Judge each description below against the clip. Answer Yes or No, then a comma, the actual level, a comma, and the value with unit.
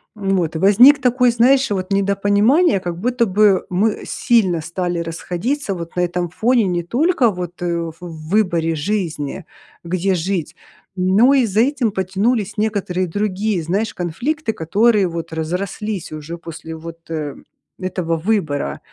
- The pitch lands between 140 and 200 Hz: Yes, high, 190 Hz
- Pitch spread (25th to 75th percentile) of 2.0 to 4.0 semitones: No, average, 4.4 semitones